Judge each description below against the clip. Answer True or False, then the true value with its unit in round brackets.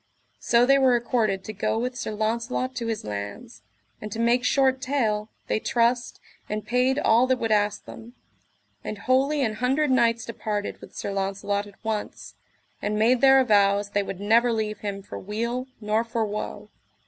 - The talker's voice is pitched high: True (225 Hz)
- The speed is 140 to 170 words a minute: False (180 wpm)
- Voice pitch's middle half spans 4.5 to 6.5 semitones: False (3.2 semitones)